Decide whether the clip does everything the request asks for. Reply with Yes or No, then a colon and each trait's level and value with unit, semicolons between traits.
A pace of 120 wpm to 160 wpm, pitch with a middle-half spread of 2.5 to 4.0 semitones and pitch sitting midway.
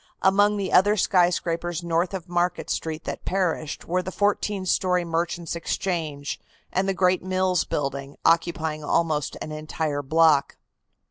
Yes: average, 140 wpm; average, 2.9 semitones; medium, 175 Hz